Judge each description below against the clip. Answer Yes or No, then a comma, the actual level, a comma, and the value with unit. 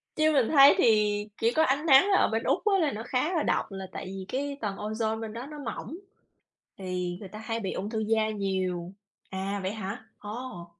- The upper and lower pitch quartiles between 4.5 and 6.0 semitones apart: Yes, wide, 5.4 semitones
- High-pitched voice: Yes, high, 220 Hz